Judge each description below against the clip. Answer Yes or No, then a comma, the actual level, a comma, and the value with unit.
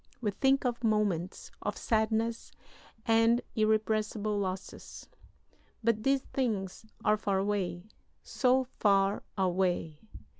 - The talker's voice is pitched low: No, high, 215 Hz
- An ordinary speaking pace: No, slow, 105 wpm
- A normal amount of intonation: Yes, average, 3.0 semitones